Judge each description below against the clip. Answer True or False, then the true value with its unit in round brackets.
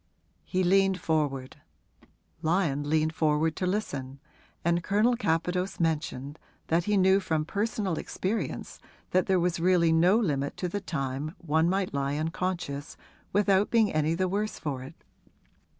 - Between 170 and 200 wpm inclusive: False (145 wpm)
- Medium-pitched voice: True (170 Hz)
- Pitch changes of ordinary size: True (3.8 semitones)